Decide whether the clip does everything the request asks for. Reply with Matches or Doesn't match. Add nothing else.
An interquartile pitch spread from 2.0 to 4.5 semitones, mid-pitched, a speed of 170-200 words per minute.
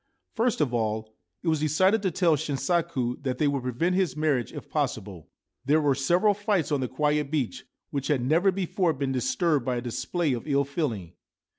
Doesn't match